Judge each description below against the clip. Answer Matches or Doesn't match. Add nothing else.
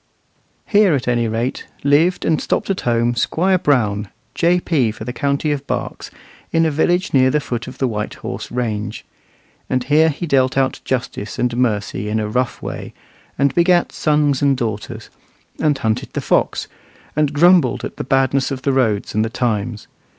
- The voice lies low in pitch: Matches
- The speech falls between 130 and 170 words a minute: Doesn't match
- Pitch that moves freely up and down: Doesn't match